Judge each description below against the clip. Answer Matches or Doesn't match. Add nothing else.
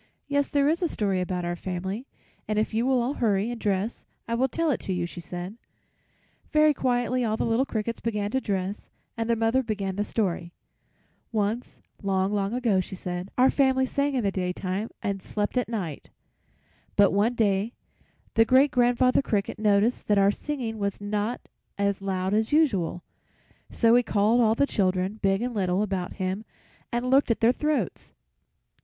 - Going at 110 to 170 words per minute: Doesn't match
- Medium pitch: Doesn't match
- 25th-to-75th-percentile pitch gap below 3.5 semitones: Doesn't match